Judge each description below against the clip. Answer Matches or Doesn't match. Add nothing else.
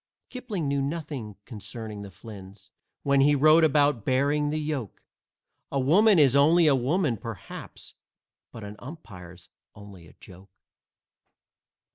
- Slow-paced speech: Matches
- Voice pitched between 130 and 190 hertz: Matches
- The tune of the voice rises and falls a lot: Matches